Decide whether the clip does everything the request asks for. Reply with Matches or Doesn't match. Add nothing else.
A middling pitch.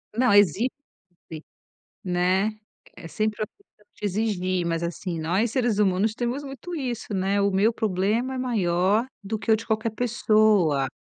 Doesn't match